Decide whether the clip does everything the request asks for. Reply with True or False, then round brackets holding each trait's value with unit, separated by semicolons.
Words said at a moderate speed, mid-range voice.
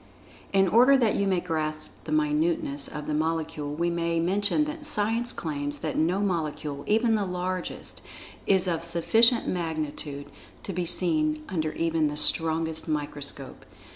True (155 wpm; 165 Hz)